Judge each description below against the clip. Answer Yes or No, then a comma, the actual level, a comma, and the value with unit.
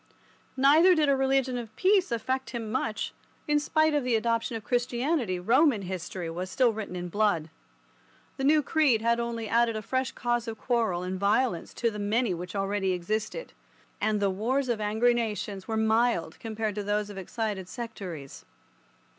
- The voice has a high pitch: Yes, high, 225 Hz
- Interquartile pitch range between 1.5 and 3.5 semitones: No, average, 3.9 semitones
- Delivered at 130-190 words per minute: Yes, average, 180 wpm